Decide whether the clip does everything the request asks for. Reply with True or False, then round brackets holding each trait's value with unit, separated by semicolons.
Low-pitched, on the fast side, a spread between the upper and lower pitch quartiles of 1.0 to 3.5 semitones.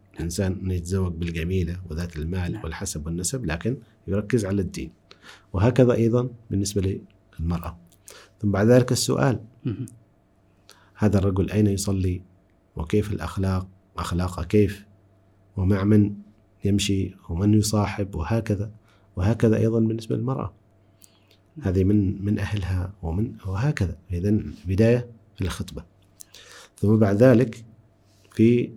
False (100 Hz; 110 wpm; 2.5 semitones)